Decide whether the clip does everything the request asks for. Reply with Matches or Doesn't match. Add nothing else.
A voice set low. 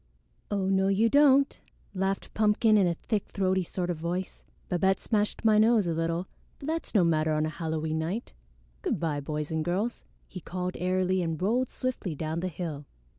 Doesn't match